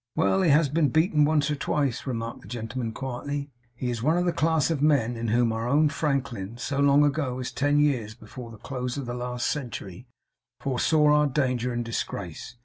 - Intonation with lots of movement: No, average, 3.6 semitones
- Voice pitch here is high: No, low, 135 Hz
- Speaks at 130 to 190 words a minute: No, fast, 205 wpm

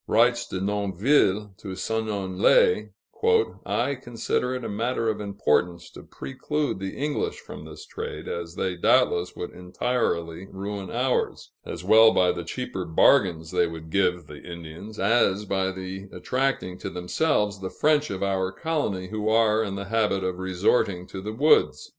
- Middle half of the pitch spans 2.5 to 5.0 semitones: Yes, average, 4.0 semitones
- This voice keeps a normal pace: Yes, average, 155 wpm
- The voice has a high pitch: No, low, 100 Hz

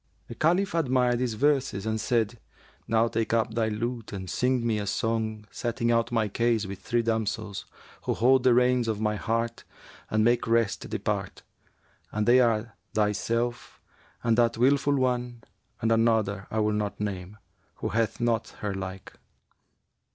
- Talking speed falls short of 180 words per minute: Yes, average, 160 wpm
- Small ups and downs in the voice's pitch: Yes, narrow, 2.0 semitones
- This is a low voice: Yes, low, 115 Hz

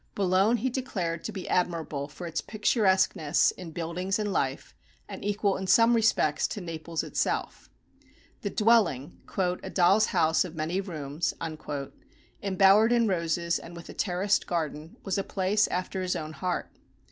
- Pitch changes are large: No, average, 3.5 semitones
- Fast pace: No, average, 155 wpm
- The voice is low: No, medium, 185 Hz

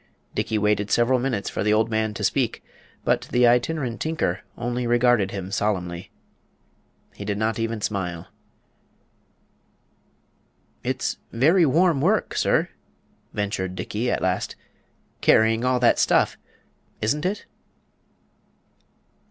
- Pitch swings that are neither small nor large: Yes, average, 3.5 semitones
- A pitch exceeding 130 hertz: No, low, 115 Hz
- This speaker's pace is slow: Yes, slow, 120 wpm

